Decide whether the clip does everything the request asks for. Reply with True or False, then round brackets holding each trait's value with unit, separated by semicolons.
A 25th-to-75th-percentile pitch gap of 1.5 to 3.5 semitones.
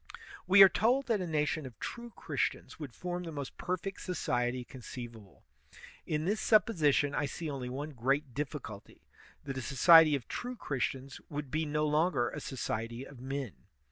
False (4.9 semitones)